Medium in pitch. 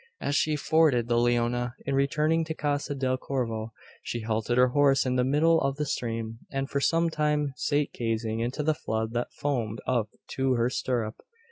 No: low, 130 Hz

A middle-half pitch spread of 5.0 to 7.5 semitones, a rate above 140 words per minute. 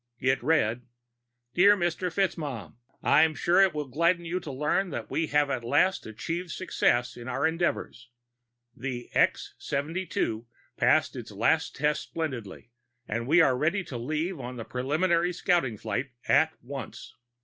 Yes: wide, 5.4 semitones; average, 155 wpm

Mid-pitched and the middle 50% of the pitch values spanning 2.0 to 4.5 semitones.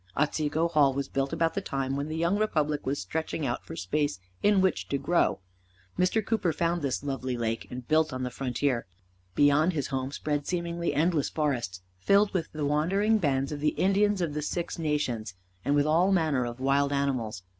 Yes: medium, 150 Hz; average, 3.9 semitones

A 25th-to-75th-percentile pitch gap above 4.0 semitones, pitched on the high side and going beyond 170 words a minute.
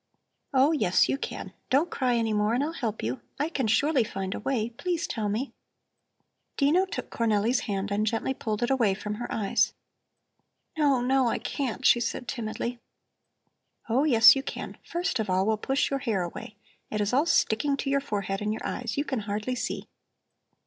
Yes: average, 4.5 semitones; high, 235 Hz; average, 190 wpm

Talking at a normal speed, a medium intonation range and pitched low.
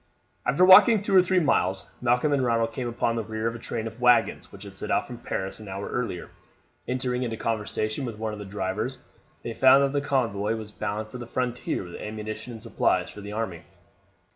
No: fast, 215 wpm; average, 3.0 semitones; low, 115 Hz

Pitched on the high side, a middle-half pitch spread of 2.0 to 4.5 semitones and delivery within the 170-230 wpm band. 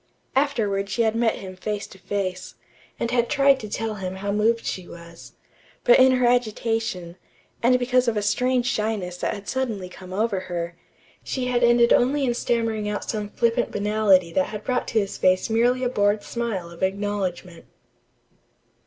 Yes: high, 215 Hz; average, 4.0 semitones; average, 180 wpm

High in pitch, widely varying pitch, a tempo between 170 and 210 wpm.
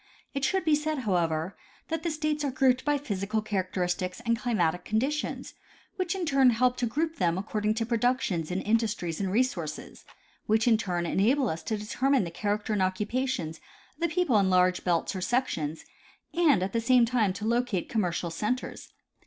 Yes: high, 220 Hz; wide, 5.9 semitones; average, 180 wpm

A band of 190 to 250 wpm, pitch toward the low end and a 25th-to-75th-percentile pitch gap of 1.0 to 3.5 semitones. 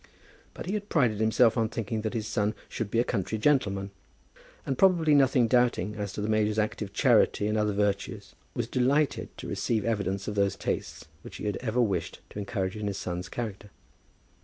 Yes: average, 195 wpm; low, 110 Hz; average, 3.2 semitones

